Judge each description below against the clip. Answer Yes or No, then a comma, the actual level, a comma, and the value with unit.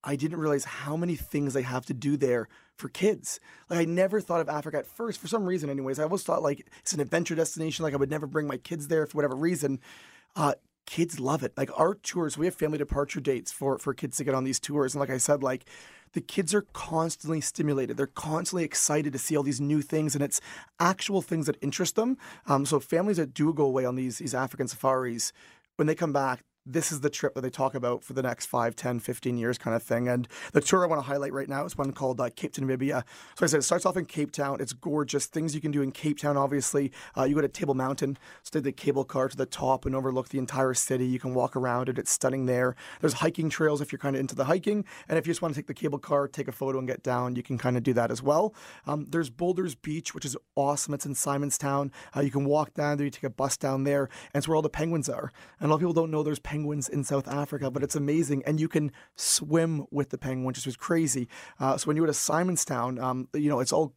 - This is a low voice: No, medium, 145 Hz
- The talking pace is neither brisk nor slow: No, fast, 270 wpm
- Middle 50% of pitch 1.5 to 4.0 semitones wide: Yes, average, 2.9 semitones